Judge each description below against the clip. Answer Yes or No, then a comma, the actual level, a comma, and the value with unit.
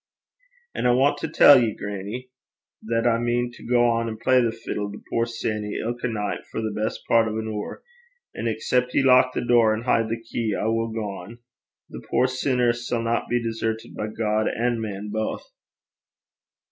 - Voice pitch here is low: Yes, low, 115 Hz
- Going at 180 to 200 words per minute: Yes, average, 185 wpm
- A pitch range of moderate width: No, narrow, 1.8 semitones